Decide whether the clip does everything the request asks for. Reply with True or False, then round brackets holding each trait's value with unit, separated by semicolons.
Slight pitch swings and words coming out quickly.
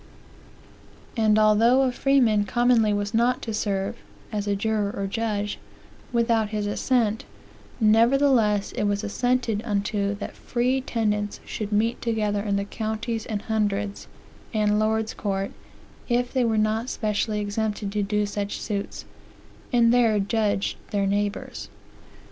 False (2.0 semitones; 135 wpm)